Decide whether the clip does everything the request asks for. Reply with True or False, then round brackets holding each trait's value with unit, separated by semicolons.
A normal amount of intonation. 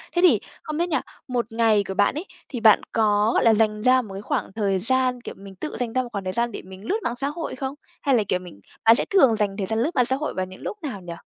True (4.3 semitones)